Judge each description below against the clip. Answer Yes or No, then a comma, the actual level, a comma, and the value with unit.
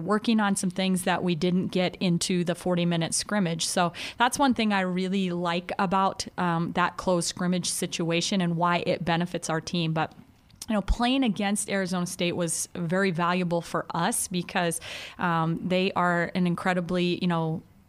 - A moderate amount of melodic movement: No, narrow, 1.9 semitones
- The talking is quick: No, average, 175 wpm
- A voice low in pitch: No, medium, 180 Hz